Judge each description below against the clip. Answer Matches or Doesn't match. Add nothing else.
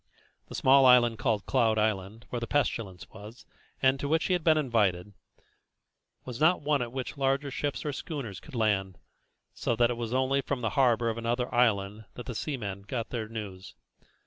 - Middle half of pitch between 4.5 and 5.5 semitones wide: Doesn't match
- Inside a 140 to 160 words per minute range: Doesn't match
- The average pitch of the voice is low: Matches